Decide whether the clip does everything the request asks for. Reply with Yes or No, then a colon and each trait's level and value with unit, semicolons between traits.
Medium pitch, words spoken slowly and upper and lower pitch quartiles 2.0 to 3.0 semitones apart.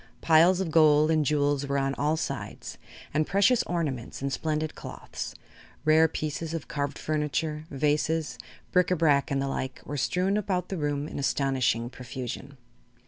No: medium, 150 Hz; average, 160 wpm; average, 2.7 semitones